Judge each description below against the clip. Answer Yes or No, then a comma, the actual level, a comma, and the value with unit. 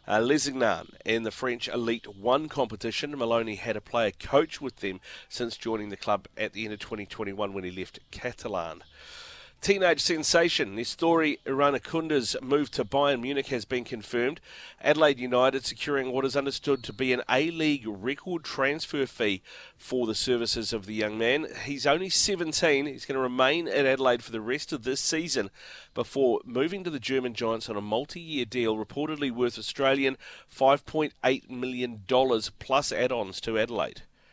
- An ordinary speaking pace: Yes, average, 165 wpm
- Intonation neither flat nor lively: Yes, average, 3.9 semitones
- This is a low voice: Yes, low, 130 Hz